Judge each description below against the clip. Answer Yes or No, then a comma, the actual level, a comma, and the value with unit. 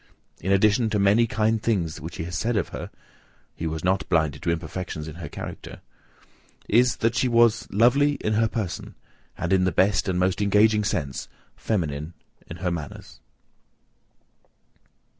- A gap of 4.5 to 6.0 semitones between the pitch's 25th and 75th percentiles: Yes, average, 4.8 semitones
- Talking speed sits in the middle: Yes, average, 160 wpm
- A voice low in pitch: Yes, low, 100 Hz